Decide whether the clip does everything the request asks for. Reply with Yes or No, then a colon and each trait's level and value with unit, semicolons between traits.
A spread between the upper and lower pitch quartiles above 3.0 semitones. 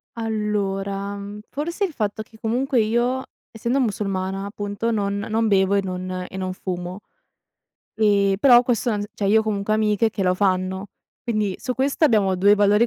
No: narrow, 2.4 semitones